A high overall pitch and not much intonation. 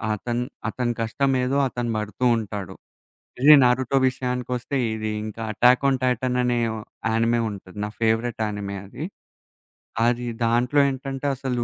No: low, 120 Hz; narrow, 2.3 semitones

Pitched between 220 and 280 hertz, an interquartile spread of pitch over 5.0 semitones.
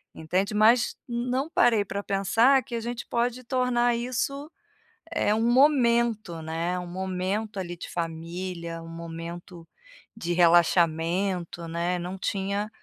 No: high, 195 Hz; wide, 5.6 semitones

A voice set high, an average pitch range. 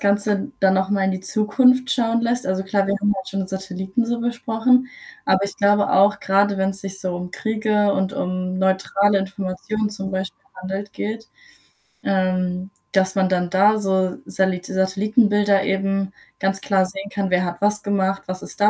No: high, 195 Hz; narrow, 1.5 semitones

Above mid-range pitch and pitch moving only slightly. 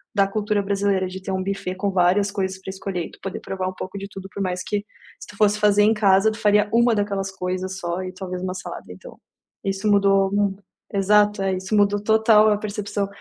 Yes: high, 195 Hz; narrow, 1.6 semitones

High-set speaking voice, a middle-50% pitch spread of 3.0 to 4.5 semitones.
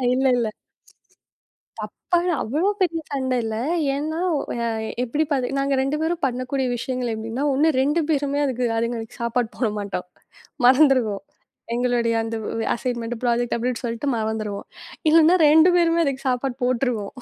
Yes: very high, 255 Hz; average, 3.7 semitones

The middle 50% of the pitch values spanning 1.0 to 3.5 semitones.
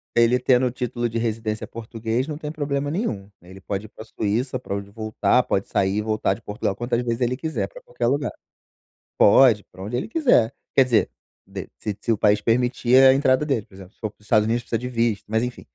Yes: average, 3.2 semitones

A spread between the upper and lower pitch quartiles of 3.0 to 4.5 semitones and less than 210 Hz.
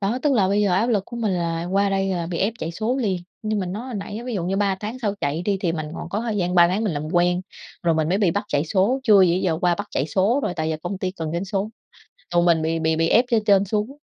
Yes: average, 3.7 semitones; high, 190 Hz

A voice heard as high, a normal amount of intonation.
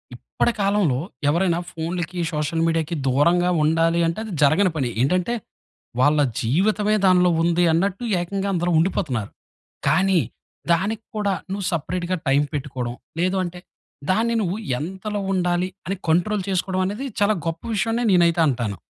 No: medium, 175 Hz; average, 3.3 semitones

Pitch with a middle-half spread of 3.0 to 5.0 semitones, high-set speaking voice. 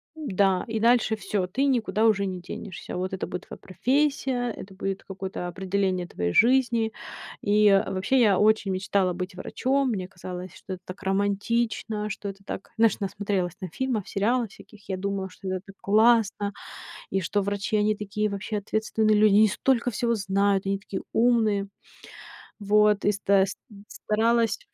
No: narrow, 2.5 semitones; high, 205 Hz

